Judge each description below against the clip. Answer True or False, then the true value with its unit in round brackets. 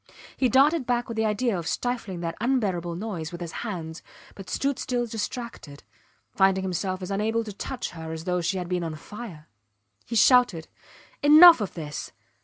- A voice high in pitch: True (200 Hz)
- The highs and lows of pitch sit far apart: True (5.7 semitones)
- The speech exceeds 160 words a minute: True (180 wpm)